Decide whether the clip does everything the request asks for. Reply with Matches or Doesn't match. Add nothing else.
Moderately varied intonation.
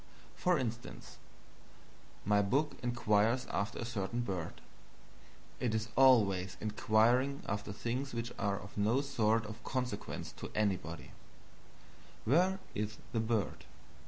Matches